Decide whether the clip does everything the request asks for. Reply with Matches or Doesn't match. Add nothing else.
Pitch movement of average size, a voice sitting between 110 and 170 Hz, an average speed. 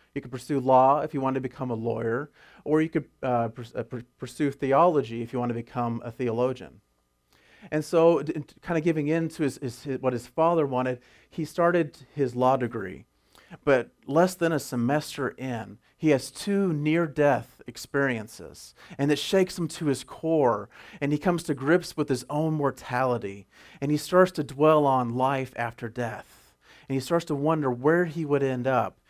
Matches